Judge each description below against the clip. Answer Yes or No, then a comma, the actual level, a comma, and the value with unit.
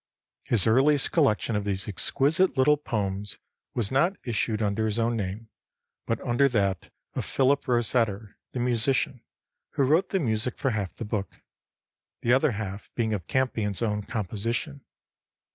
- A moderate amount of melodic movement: Yes, average, 4.1 semitones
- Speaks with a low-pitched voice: Yes, low, 115 Hz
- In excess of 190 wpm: No, average, 150 wpm